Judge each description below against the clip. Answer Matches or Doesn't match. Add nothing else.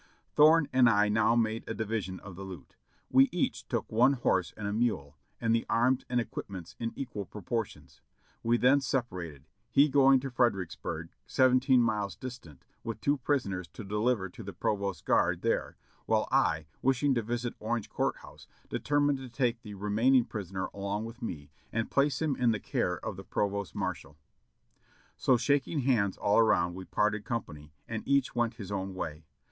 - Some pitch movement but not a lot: Matches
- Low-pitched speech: Matches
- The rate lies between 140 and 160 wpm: Doesn't match